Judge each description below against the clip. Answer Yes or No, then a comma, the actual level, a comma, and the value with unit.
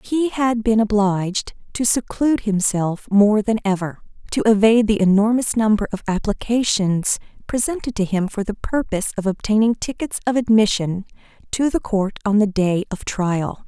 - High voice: Yes, high, 210 Hz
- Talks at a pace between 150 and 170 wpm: Yes, average, 160 wpm